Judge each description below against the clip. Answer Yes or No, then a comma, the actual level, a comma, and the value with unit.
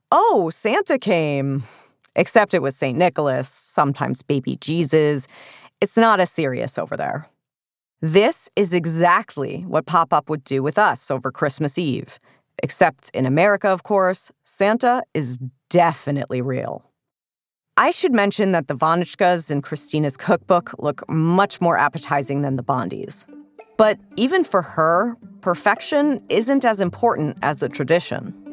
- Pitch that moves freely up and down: Yes, wide, 6.0 semitones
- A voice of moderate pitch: Yes, medium, 170 Hz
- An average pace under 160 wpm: Yes, average, 140 wpm